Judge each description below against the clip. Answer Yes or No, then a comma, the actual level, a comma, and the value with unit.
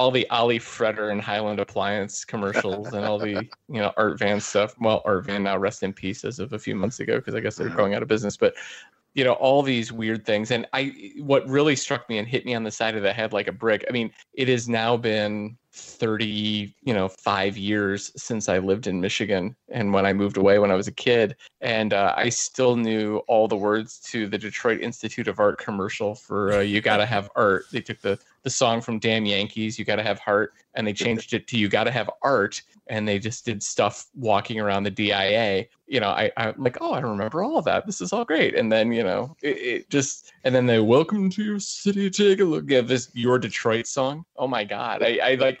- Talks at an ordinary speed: No, fast, 240 wpm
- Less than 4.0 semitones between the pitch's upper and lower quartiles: Yes, average, 3.3 semitones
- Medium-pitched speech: No, low, 110 Hz